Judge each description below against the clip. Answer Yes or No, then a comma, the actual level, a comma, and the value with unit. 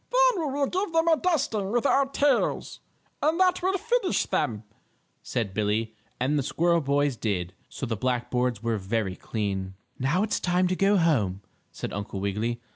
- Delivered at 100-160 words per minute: No, average, 180 wpm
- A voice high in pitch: No, medium, 140 Hz